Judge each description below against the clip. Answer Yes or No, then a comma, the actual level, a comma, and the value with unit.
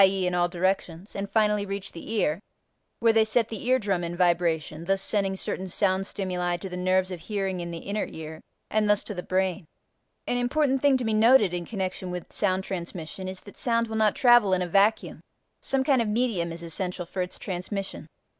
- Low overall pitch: No, high, 190 Hz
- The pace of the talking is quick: Yes, fast, 215 wpm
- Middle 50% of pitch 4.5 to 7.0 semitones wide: No, average, 3.3 semitones